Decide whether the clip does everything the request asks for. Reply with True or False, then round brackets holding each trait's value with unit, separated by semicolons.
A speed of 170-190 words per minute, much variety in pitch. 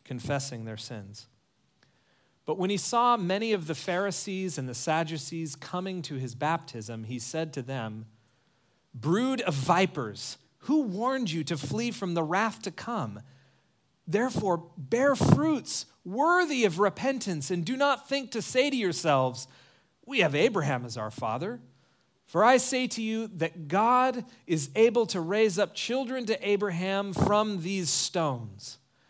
False (150 wpm; 8.6 semitones)